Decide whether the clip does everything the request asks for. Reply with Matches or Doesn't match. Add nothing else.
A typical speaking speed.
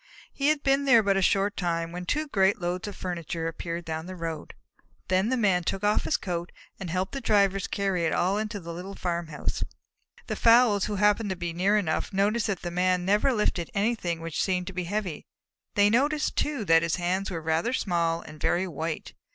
Doesn't match